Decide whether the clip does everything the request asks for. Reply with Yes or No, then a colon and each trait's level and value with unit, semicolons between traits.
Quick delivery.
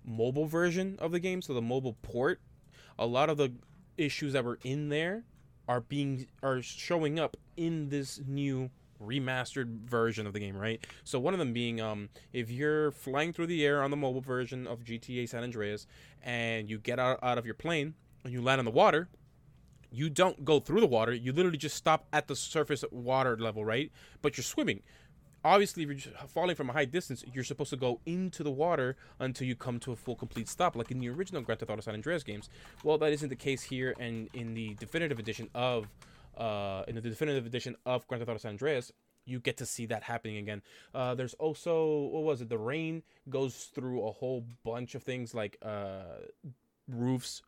Yes: fast, 210 wpm